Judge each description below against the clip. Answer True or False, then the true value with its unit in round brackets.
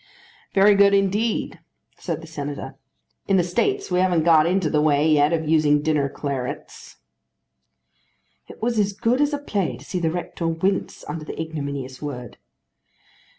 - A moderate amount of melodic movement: True (4.9 semitones)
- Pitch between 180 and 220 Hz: False (165 Hz)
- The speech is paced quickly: False (160 wpm)